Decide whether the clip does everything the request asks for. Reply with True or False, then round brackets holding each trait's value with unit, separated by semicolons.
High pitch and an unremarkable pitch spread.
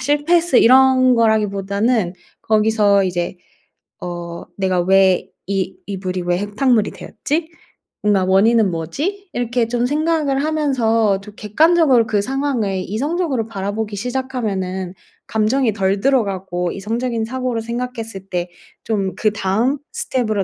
True (220 Hz; 4.9 semitones)